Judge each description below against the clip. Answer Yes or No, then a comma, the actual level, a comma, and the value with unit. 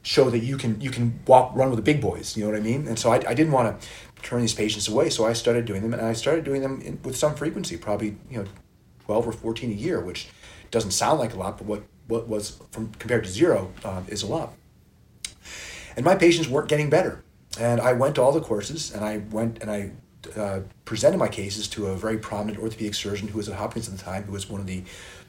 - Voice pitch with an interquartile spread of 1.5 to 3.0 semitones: Yes, average, 2.7 semitones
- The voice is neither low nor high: No, low, 110 Hz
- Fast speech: Yes, fast, 255 wpm